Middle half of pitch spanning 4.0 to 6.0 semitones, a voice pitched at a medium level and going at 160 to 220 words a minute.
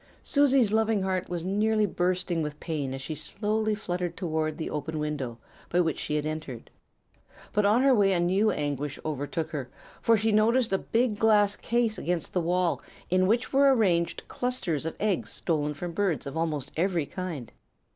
Yes: wide, 5.5 semitones; medium, 180 Hz; average, 180 wpm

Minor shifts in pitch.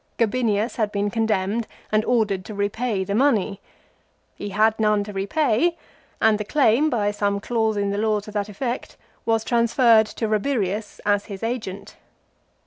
Yes: narrow, 2.3 semitones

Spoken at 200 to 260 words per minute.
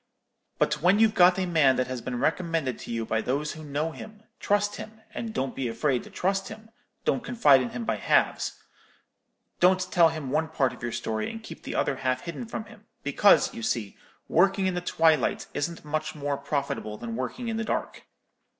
Yes: fast, 205 wpm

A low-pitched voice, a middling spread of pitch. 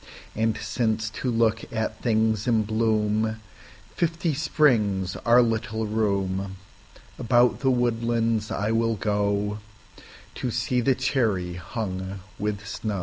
No: low, 110 Hz; narrow, 2.3 semitones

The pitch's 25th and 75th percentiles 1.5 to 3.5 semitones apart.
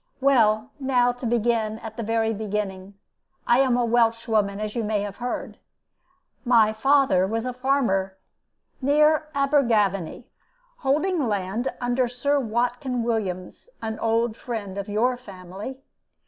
Yes: average, 3.2 semitones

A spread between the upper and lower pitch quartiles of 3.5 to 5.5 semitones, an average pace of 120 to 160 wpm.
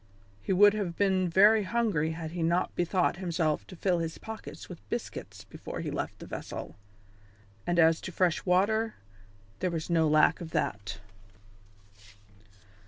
No: average, 3.1 semitones; average, 155 wpm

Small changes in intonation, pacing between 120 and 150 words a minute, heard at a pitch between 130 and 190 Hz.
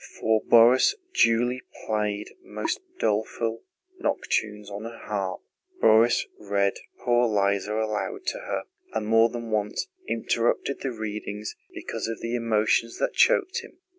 No: narrow, 2.0 semitones; slow, 135 wpm; low, 110 Hz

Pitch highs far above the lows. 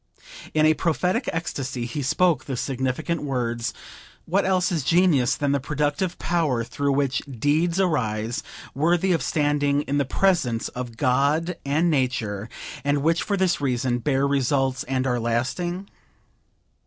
No: average, 4.7 semitones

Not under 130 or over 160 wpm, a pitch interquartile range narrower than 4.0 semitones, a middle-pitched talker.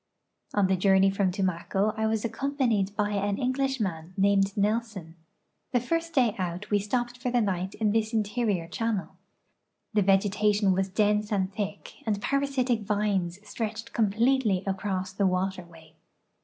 No: average, 150 wpm; average, 2.8 semitones; high, 205 Hz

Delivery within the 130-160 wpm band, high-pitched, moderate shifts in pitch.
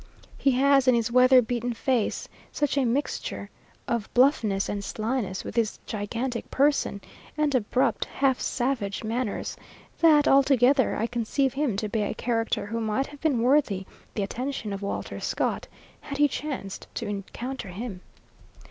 Yes: average, 155 wpm; high, 245 Hz; average, 4.1 semitones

